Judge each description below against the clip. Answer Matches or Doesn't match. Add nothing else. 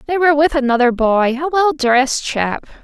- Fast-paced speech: Doesn't match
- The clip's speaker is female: Matches